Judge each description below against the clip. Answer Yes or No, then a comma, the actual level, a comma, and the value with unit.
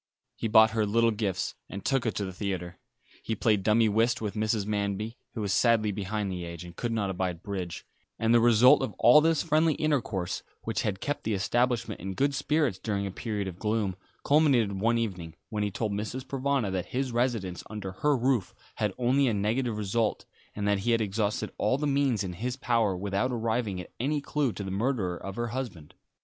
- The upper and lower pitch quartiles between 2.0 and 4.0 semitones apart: Yes, average, 3.7 semitones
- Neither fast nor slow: No, fast, 210 wpm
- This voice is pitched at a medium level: No, low, 110 Hz